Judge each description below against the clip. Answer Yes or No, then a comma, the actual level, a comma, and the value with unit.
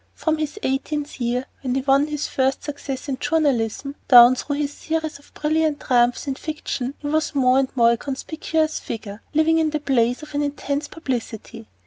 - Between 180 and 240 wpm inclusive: Yes, average, 185 wpm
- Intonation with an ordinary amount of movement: Yes, average, 3.1 semitones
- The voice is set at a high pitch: Yes, very high, 280 Hz